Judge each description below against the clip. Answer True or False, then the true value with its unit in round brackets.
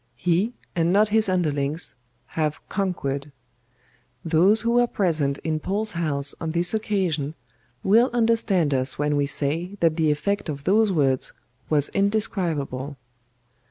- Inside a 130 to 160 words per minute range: True (135 wpm)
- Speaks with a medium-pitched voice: True (165 Hz)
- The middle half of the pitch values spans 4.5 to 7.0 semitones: True (5.4 semitones)